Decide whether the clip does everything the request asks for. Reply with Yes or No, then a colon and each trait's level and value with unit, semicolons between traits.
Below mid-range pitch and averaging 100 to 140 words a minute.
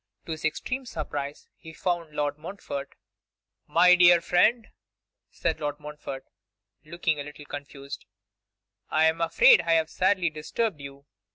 No: medium, 160 Hz; slow, 135 wpm